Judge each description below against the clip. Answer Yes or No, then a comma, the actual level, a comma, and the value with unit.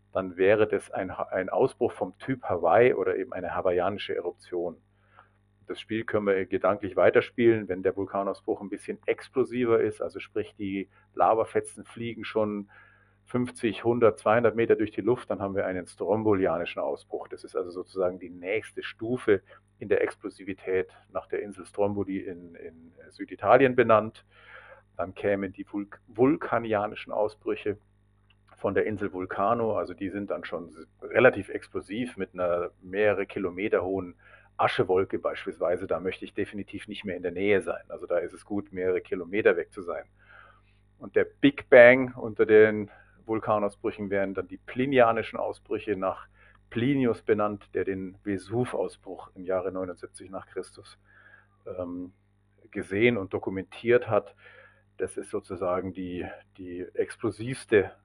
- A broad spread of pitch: No, average, 3.8 semitones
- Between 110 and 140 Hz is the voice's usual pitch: No, low, 100 Hz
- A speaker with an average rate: Yes, average, 145 wpm